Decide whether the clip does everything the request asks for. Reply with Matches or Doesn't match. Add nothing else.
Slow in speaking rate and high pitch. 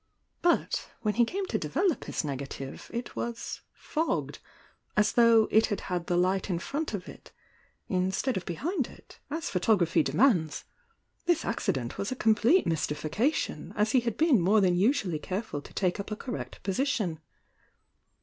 Doesn't match